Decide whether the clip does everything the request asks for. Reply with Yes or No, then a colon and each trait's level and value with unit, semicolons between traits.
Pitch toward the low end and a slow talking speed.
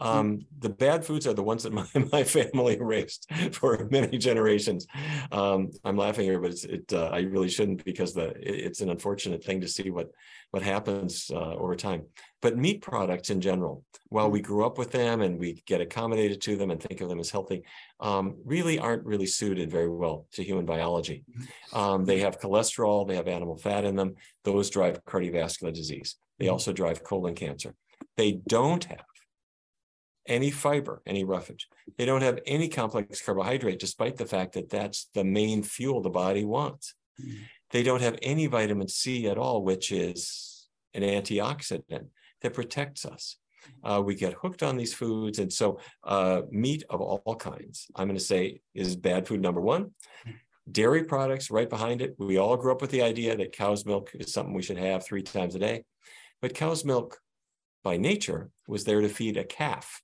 No: low, 105 Hz; average, 190 wpm